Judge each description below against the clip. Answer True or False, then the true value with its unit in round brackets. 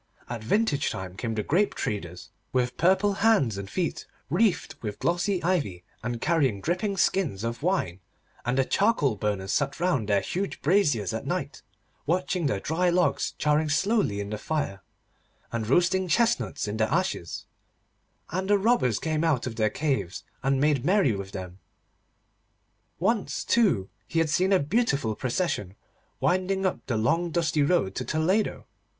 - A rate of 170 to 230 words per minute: False (160 wpm)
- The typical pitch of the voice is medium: True (150 Hz)